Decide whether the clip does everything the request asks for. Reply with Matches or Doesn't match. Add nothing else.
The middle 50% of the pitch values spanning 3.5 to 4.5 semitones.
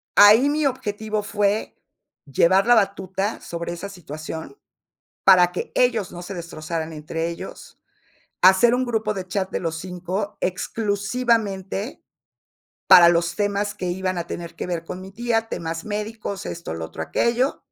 Matches